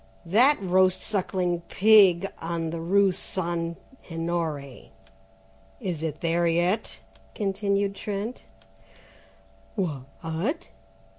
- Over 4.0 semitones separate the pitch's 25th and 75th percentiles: No, average, 3.1 semitones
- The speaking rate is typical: No, slow, 90 wpm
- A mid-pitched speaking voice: Yes, medium, 180 Hz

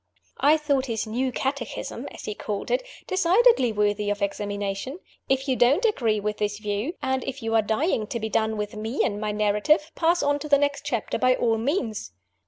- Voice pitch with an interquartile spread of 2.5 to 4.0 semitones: No, average, 5.2 semitones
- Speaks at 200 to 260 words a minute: Yes, fast, 205 wpm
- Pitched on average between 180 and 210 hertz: No, high, 235 Hz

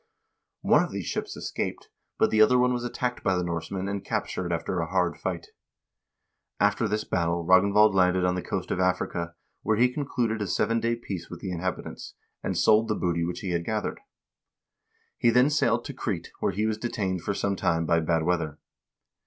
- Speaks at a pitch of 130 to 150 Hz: No, very low, 95 Hz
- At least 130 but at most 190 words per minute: No, average, 200 wpm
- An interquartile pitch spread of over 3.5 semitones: Yes, average, 4.0 semitones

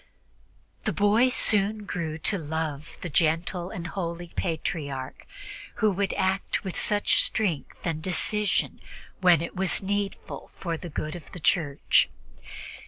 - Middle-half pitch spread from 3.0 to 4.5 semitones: Yes, average, 3.7 semitones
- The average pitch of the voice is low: No, medium, 175 Hz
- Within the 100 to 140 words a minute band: Yes, slow, 135 wpm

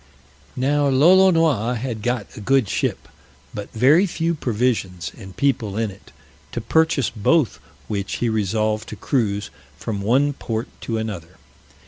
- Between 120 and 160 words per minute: Yes, average, 140 wpm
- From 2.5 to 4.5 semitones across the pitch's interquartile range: No, average, 5.2 semitones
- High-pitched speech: No, low, 115 Hz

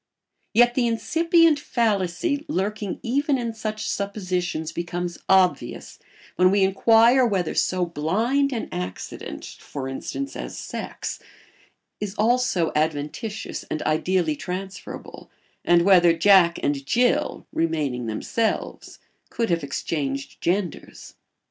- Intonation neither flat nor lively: No, wide, 5.7 semitones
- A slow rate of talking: Yes, slow, 110 wpm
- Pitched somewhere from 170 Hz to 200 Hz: Yes, high, 190 Hz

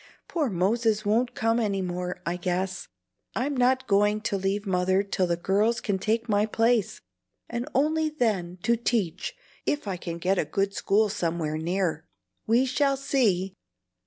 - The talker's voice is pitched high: Yes, high, 205 Hz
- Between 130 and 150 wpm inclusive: No, average, 160 wpm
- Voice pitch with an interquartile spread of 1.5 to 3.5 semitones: No, average, 4.3 semitones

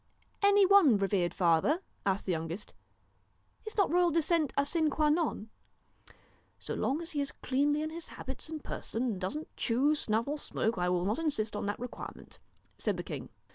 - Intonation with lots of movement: Yes, wide, 7.3 semitones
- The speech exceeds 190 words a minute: Yes, average, 200 wpm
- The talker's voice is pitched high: Yes, very high, 280 Hz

